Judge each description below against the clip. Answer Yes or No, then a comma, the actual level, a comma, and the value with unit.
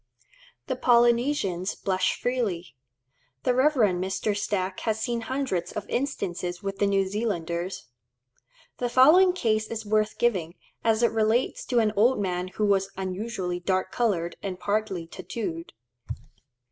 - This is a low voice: No, high, 205 Hz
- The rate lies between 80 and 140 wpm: Yes, slow, 135 wpm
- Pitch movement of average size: Yes, average, 4.2 semitones